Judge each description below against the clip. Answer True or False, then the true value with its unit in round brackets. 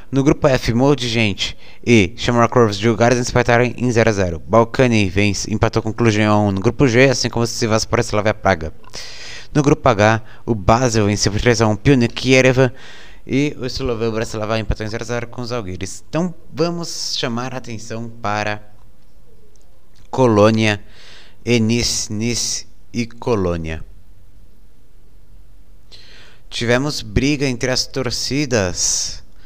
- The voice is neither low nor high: False (115 Hz)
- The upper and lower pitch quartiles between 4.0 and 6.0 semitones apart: False (2.8 semitones)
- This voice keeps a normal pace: True (145 wpm)